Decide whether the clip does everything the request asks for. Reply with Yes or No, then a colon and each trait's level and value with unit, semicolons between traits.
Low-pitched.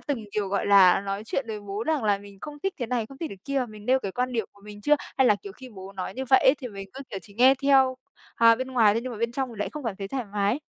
No: high, 230 Hz